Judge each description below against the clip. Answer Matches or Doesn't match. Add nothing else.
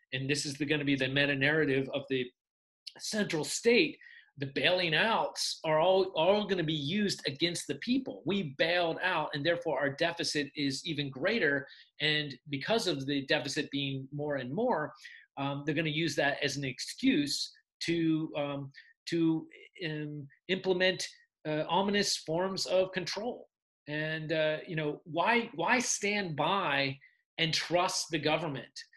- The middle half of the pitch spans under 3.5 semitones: Doesn't match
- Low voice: Doesn't match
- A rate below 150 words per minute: Doesn't match